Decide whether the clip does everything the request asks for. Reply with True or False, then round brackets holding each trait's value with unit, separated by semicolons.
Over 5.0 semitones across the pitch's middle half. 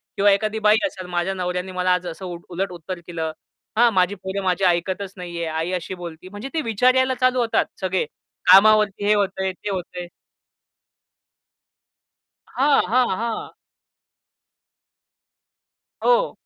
False (3.2 semitones)